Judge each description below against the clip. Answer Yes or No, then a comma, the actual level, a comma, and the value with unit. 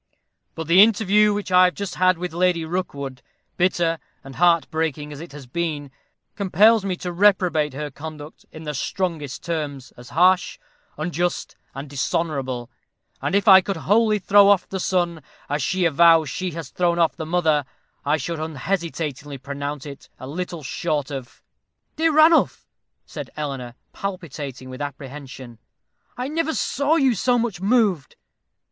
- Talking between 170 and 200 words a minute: No, average, 160 wpm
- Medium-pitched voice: Yes, medium, 165 Hz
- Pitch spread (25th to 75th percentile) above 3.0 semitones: Yes, average, 4.6 semitones